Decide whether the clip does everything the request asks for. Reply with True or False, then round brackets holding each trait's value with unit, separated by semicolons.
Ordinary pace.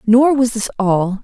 True (195 wpm)